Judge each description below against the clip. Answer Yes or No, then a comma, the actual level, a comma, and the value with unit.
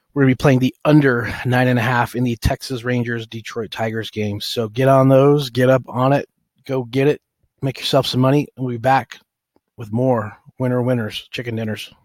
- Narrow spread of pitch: Yes, narrow, 2.1 semitones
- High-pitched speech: No, low, 125 Hz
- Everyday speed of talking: No, fast, 220 wpm